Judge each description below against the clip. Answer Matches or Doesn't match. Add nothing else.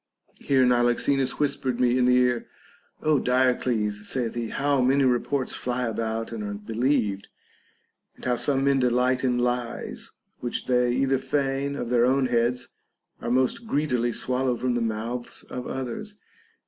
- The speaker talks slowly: Doesn't match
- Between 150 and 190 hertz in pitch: Doesn't match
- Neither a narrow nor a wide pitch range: Doesn't match